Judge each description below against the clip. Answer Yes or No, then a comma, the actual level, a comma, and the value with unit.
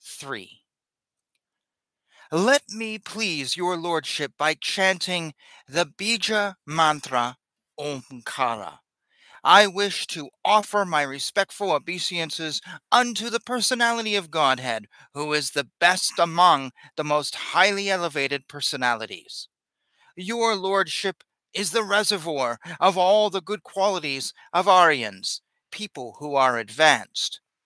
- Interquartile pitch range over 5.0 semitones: Yes, wide, 5.6 semitones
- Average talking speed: No, slow, 110 wpm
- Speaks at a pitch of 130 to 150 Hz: No, medium, 175 Hz